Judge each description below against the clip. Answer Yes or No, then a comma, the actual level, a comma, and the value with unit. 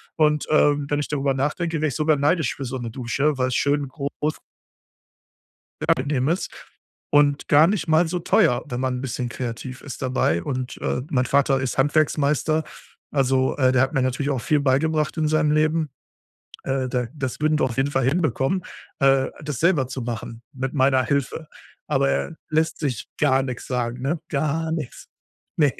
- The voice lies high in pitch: No, medium, 140 Hz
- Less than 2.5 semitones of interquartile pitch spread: No, average, 2.9 semitones